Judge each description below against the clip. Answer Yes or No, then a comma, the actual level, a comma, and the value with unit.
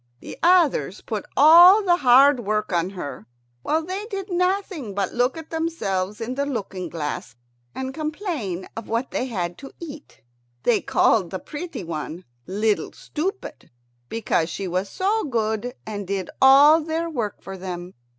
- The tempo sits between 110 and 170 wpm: Yes, average, 160 wpm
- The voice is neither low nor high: No, high, 240 Hz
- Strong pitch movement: Yes, wide, 8.9 semitones